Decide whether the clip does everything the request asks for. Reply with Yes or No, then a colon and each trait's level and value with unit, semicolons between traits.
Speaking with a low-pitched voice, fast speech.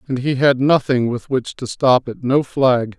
Yes: low, 130 Hz; fast, 220 wpm